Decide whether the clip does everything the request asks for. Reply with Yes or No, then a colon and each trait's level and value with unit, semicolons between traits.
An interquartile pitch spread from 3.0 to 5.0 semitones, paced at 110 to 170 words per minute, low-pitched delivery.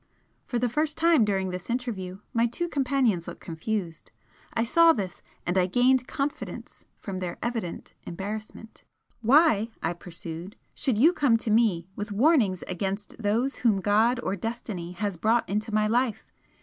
No: average, 4.6 semitones; average, 160 wpm; high, 215 Hz